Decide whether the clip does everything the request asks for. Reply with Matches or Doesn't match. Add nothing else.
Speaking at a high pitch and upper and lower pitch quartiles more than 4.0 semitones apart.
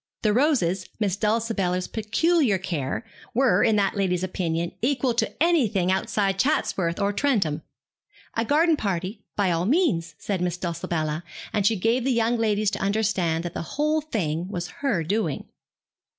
Matches